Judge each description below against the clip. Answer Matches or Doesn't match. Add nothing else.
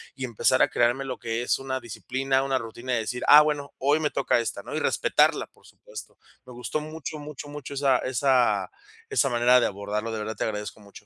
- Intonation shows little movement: Doesn't match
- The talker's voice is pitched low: Matches